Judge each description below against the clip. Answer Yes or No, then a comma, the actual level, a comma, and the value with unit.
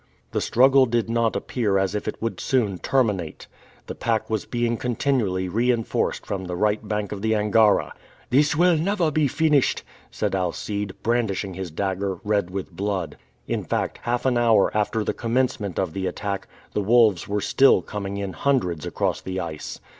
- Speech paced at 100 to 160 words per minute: No, average, 175 wpm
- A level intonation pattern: No, average, 3.8 semitones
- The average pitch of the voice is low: Yes, low, 105 Hz